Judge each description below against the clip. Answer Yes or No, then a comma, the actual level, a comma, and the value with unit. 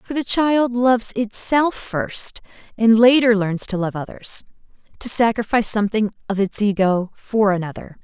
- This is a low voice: No, high, 220 Hz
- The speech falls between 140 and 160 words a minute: Yes, average, 150 wpm